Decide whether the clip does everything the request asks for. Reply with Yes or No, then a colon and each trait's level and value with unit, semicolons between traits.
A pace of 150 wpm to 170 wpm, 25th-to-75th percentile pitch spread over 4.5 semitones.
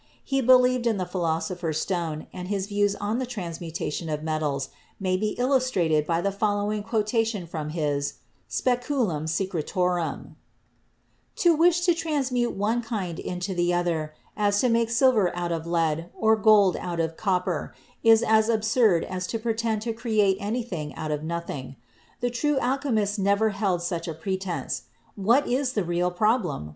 Yes: average, 160 wpm; average, 5.1 semitones